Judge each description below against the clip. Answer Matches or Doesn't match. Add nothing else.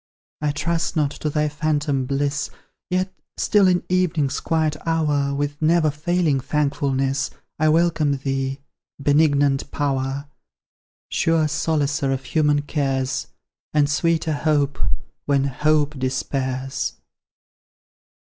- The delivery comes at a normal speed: Doesn't match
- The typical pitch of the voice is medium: Matches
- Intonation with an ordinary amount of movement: Doesn't match